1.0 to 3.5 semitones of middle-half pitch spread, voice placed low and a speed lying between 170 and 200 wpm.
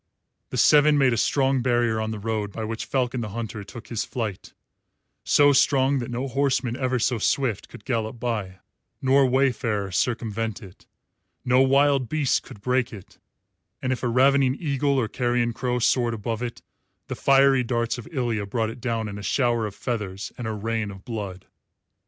Yes: average, 3.0 semitones; low, 120 Hz; average, 180 wpm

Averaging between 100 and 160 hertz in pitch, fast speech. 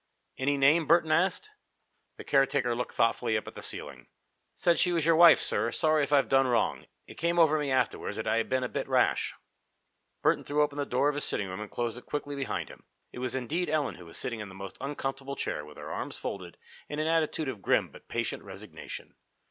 Yes: medium, 140 Hz; fast, 225 wpm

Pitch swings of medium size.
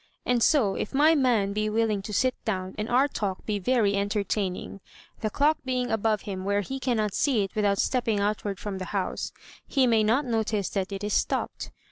Yes: average, 3.7 semitones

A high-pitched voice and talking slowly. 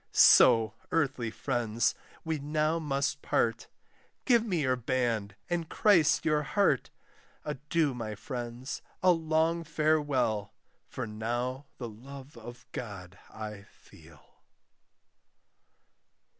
No: low, 135 Hz; slow, 105 wpm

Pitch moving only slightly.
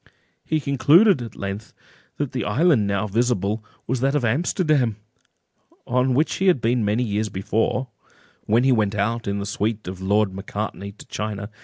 No: average, 4.1 semitones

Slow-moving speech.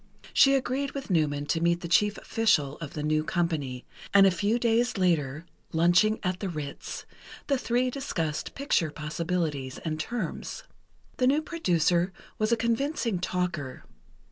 No: average, 150 wpm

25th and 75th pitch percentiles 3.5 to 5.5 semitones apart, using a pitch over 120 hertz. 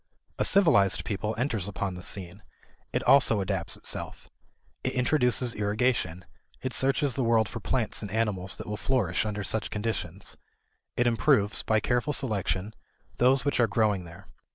No: average, 3.9 semitones; low, 110 Hz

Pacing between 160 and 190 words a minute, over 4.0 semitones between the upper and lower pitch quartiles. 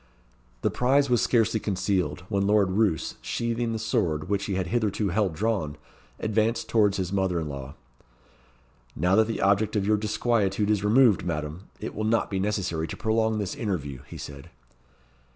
No: average, 170 wpm; average, 3.3 semitones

